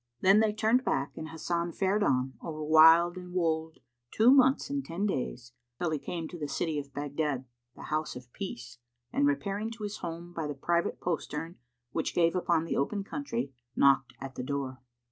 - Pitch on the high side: No, medium, 165 Hz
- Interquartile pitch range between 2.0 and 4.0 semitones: No, wide, 5.4 semitones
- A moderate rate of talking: Yes, average, 190 wpm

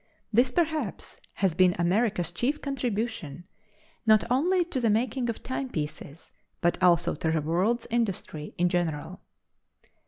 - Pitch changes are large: Yes, wide, 6.2 semitones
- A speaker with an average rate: No, slow, 130 wpm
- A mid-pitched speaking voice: No, high, 205 Hz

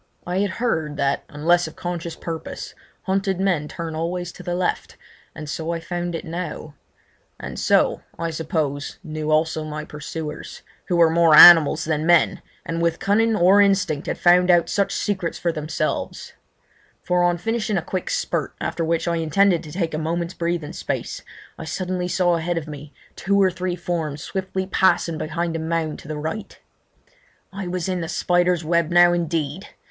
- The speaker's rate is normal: Yes, average, 180 wpm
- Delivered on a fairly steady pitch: Yes, narrow, 2.2 semitones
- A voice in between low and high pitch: Yes, medium, 170 Hz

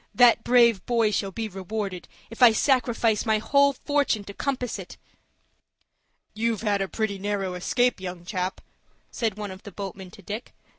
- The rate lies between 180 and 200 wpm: No, average, 165 wpm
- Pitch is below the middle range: No, high, 215 Hz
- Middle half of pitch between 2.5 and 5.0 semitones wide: Yes, average, 3.4 semitones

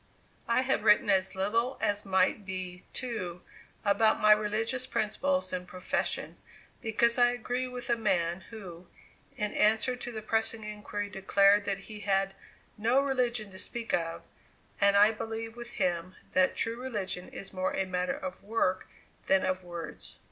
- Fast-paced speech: No, average, 160 wpm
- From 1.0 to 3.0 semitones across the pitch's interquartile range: No, average, 3.4 semitones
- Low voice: No, high, 210 Hz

